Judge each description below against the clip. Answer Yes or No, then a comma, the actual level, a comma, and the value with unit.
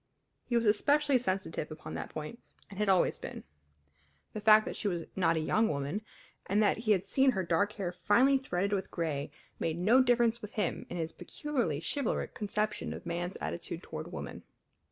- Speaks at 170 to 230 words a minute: Yes, average, 190 wpm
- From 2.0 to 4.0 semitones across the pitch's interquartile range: No, average, 5.1 semitones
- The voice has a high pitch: Yes, high, 200 Hz